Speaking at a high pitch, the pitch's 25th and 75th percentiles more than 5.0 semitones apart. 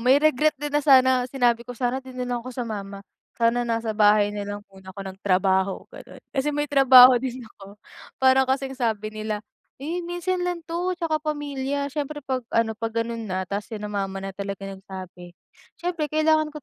Yes: high, 245 Hz; wide, 5.5 semitones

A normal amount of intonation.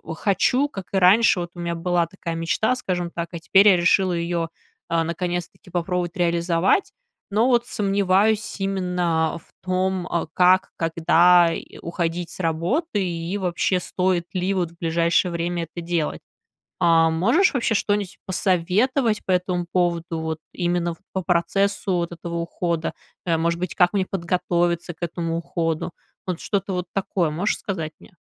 No: narrow, 2.1 semitones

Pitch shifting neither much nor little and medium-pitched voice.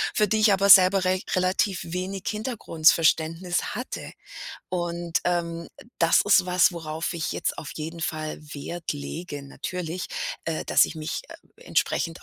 No: narrow, 2.3 semitones; medium, 175 Hz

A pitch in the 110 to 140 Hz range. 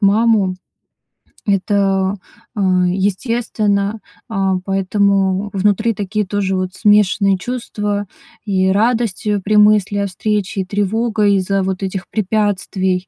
No: high, 200 Hz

